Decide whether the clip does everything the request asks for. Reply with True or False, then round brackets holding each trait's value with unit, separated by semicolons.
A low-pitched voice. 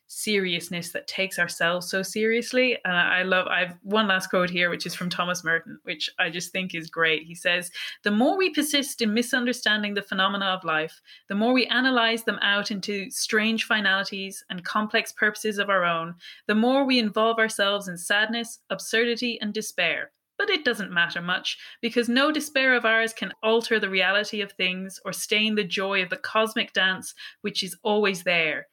False (205 Hz)